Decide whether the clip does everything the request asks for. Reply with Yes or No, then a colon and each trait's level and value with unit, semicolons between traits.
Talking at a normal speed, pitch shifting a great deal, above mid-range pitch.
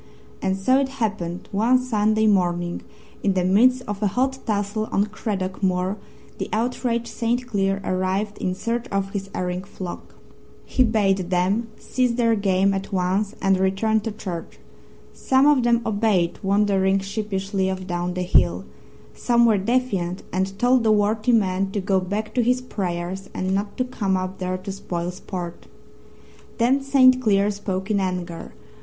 No: average, 165 wpm; average, 3.3 semitones; high, 200 Hz